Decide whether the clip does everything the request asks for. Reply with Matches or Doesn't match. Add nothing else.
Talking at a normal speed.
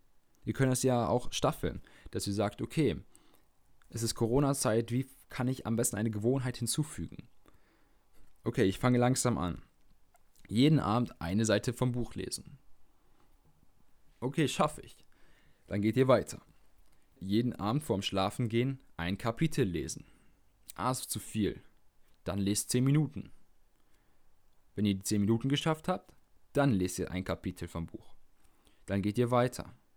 Matches